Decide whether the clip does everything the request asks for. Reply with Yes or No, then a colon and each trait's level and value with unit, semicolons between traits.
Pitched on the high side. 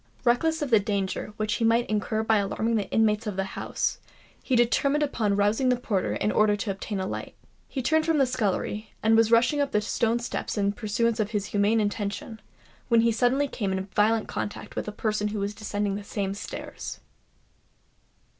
Yes: high, 215 Hz